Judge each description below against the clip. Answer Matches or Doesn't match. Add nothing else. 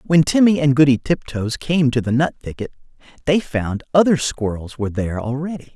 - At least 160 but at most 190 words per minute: Matches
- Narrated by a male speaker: Matches